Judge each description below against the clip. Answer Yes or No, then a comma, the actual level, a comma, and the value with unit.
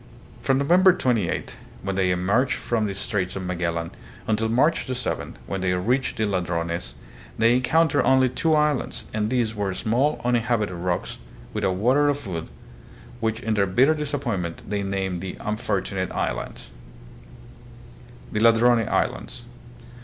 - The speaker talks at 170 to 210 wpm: No, average, 145 wpm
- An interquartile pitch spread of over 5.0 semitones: Yes, wide, 5.4 semitones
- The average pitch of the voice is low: Yes, low, 110 Hz